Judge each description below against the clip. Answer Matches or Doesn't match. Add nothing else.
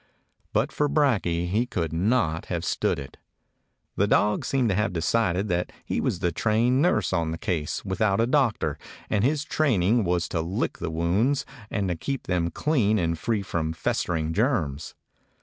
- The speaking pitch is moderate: Doesn't match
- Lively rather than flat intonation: Matches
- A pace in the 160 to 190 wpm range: Matches